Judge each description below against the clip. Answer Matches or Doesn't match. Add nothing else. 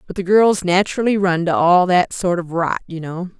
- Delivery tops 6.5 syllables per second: Doesn't match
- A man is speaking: Doesn't match